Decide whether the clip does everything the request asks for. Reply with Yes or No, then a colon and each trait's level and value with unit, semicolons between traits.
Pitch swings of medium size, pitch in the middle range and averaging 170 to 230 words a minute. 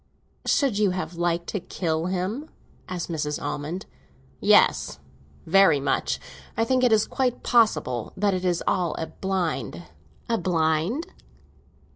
No: average, 4.7 semitones; medium, 180 Hz; slow, 135 wpm